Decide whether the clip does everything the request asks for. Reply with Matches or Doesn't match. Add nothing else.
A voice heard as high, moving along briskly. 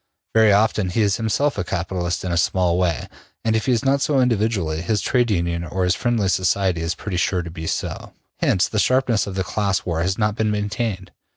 Doesn't match